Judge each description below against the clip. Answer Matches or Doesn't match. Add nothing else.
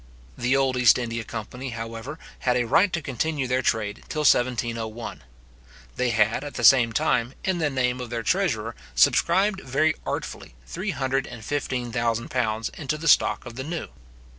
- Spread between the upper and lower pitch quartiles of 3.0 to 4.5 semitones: Matches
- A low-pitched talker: Matches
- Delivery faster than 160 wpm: Matches